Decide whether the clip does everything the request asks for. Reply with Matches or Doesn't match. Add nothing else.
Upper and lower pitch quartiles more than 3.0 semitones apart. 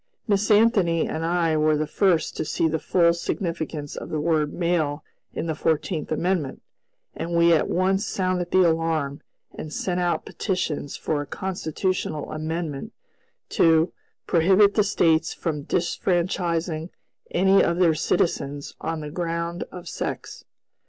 Doesn't match